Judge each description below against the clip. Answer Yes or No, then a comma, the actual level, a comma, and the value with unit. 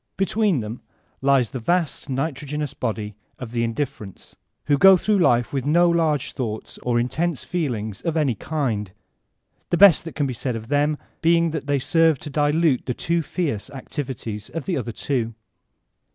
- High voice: No, medium, 140 Hz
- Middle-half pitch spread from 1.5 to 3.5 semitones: No, wide, 5.4 semitones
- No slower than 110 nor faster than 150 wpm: No, average, 175 wpm